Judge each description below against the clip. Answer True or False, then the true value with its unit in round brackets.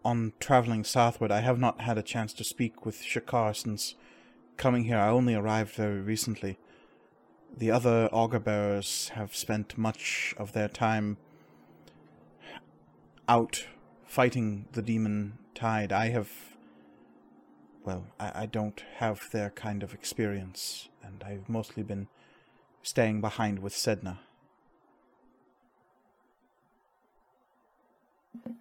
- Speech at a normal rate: False (115 wpm)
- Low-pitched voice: True (110 Hz)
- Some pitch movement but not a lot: False (2.2 semitones)